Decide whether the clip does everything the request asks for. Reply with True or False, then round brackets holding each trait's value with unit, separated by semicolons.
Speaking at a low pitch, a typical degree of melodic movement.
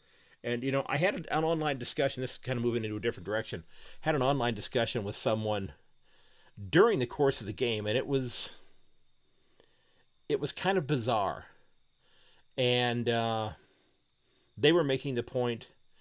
True (120 Hz; 3.5 semitones)